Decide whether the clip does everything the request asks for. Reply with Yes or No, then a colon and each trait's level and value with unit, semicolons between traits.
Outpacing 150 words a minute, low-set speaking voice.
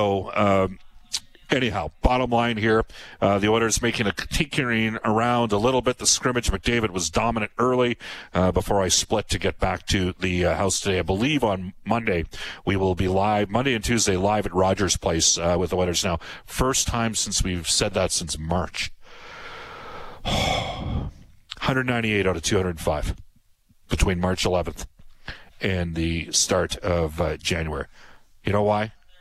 Yes: average, 160 wpm; low, 100 Hz